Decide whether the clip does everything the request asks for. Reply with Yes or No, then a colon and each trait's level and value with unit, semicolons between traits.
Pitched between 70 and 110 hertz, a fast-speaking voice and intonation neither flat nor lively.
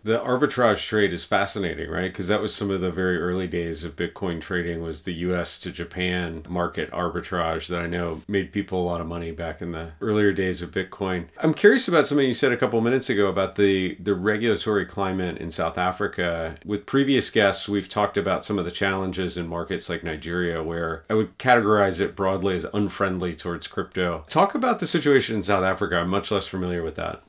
Yes: very low, 95 Hz; fast, 215 wpm; average, 3.2 semitones